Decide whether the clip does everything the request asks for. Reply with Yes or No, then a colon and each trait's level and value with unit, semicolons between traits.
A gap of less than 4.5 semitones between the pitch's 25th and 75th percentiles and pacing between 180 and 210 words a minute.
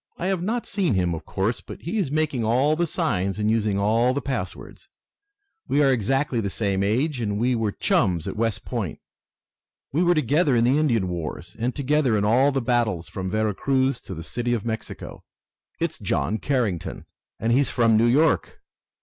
No: average, 5.2 semitones; average, 190 wpm